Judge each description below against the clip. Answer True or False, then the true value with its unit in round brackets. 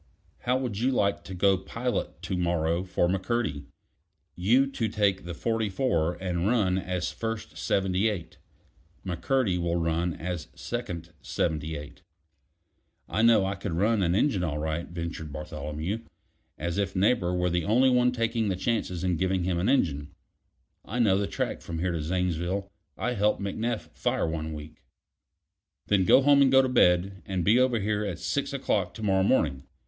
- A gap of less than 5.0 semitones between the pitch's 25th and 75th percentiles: True (4.6 semitones)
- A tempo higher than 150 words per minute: True (175 wpm)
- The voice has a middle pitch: False (95 Hz)